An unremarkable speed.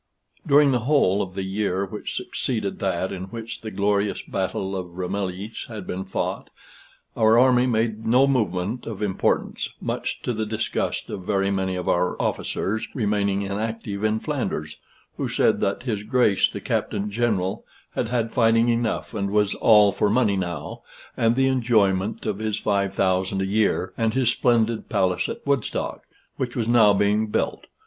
Yes: average, 170 wpm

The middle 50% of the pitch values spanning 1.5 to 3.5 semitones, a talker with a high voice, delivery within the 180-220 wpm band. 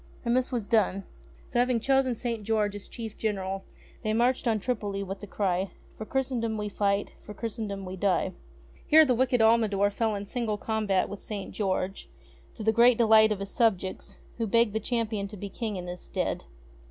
Yes: average, 2.8 semitones; high, 215 Hz; average, 195 wpm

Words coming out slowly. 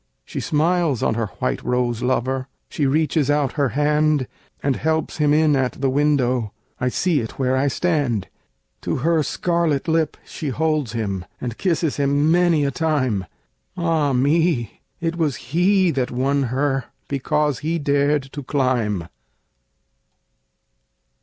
No: average, 145 wpm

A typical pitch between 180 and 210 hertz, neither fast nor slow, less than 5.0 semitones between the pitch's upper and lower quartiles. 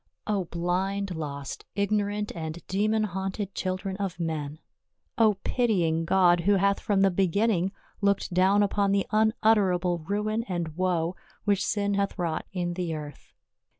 Yes: high, 190 Hz; average, 150 wpm; average, 2.7 semitones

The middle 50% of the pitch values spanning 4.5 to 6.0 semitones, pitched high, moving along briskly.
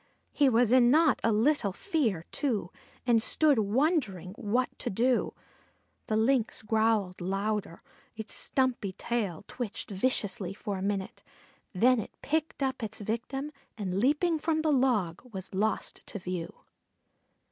No: average, 4.9 semitones; high, 225 Hz; average, 140 wpm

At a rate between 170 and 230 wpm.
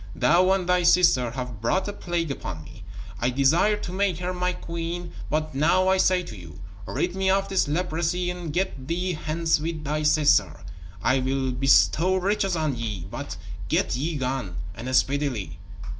Yes: average, 175 wpm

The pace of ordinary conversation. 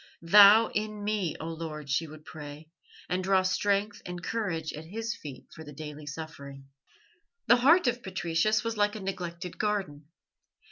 Yes: average, 160 wpm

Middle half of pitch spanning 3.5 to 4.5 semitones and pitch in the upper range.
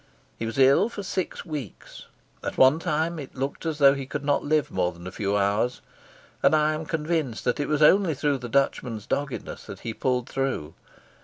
No: average, 4.0 semitones; medium, 140 Hz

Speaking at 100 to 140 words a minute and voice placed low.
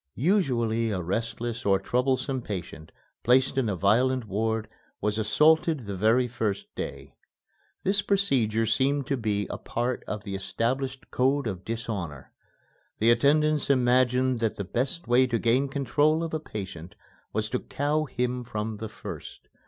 No: average, 150 wpm; low, 120 Hz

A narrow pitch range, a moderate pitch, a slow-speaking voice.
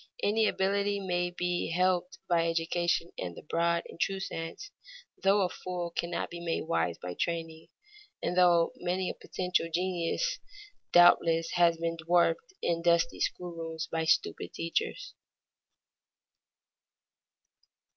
Yes: narrow, 1.6 semitones; medium, 175 Hz; slow, 130 wpm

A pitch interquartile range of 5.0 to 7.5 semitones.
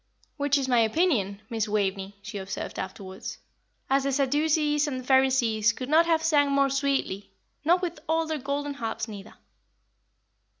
Yes: average, 5.3 semitones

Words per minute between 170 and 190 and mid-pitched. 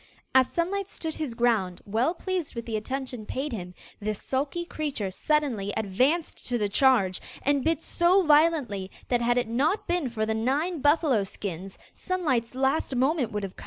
No: average, 175 wpm; very high, 260 Hz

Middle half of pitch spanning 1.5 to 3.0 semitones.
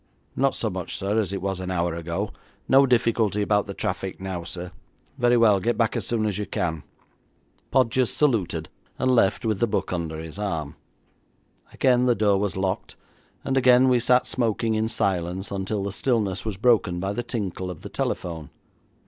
No: average, 4.2 semitones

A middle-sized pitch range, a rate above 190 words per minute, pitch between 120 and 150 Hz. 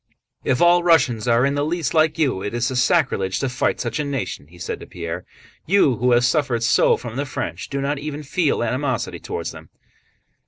Yes: average, 4.3 semitones; fast, 205 wpm; low, 135 Hz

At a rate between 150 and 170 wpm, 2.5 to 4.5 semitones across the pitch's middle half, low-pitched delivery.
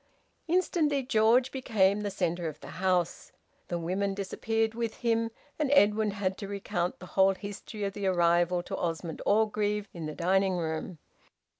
No: average, 160 wpm; average, 3.7 semitones; high, 200 Hz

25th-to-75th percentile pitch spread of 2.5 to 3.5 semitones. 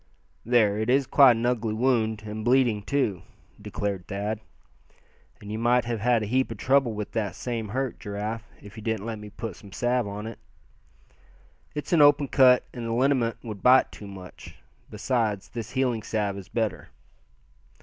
Yes: average, 3.0 semitones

